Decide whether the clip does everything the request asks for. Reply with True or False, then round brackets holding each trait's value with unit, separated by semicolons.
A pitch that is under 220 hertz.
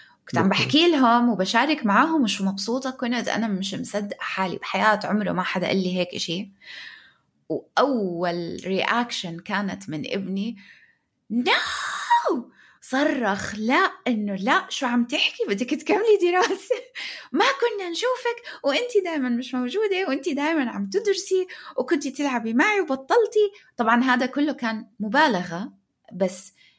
False (250 Hz)